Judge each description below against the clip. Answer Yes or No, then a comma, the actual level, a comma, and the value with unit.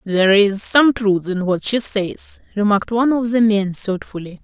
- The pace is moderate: Yes, average, 190 wpm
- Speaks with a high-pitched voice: Yes, high, 210 Hz